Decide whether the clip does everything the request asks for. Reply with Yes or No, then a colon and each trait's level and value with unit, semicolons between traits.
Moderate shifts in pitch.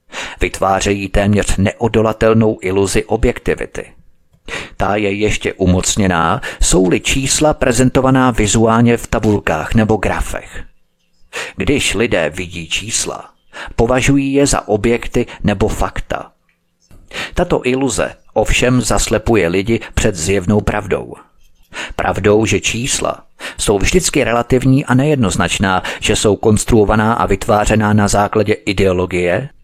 Yes: average, 3.3 semitones